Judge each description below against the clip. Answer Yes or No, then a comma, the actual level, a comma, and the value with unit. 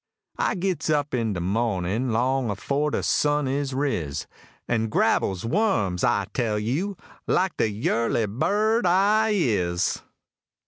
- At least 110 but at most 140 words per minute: Yes, slow, 135 wpm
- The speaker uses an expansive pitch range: Yes, wide, 7.3 semitones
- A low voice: Yes, low, 125 Hz